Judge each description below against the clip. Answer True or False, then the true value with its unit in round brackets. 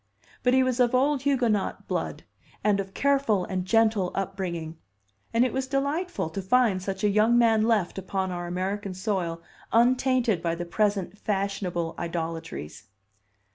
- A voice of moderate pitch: False (200 Hz)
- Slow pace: False (150 wpm)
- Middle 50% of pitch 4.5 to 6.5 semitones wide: True (5.0 semitones)